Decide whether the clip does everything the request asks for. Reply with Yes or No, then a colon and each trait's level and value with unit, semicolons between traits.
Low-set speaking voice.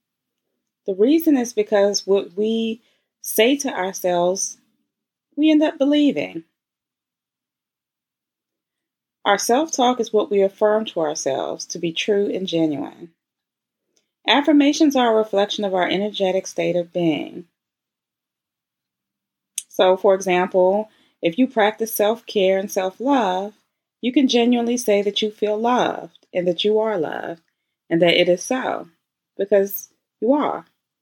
No: high, 205 Hz